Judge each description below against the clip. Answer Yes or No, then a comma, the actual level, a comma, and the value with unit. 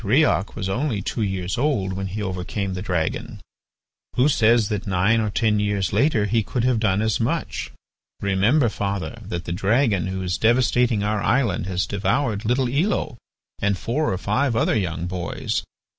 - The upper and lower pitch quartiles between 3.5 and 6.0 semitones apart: Yes, average, 4.0 semitones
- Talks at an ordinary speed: Yes, average, 175 wpm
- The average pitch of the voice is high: No, low, 105 Hz